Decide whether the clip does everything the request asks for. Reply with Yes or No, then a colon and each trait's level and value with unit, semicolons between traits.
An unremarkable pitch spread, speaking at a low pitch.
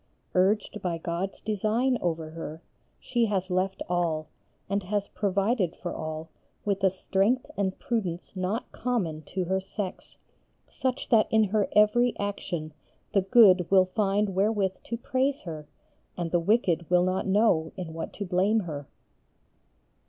No: average, 3.3 semitones; high, 190 Hz